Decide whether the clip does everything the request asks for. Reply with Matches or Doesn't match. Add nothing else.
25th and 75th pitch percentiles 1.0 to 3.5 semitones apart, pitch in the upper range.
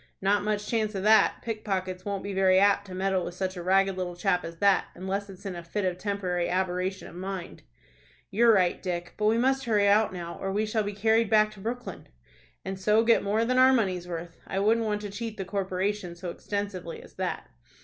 Matches